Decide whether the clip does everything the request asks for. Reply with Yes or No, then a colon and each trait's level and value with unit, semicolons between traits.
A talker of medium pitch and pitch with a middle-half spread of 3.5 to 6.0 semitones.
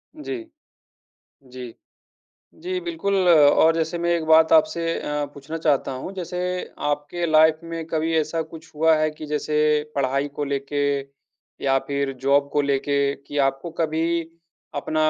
No: medium, 155 Hz; average, 2.7 semitones